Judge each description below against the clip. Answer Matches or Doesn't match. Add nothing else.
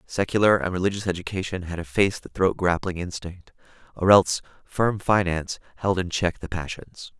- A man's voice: Matches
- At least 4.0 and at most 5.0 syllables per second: Doesn't match